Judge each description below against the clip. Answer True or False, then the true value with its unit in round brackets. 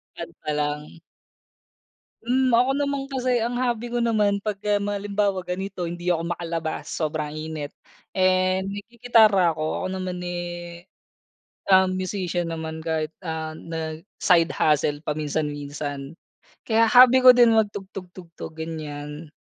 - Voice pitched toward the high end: False (175 Hz)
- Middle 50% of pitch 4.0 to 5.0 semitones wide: True (4.6 semitones)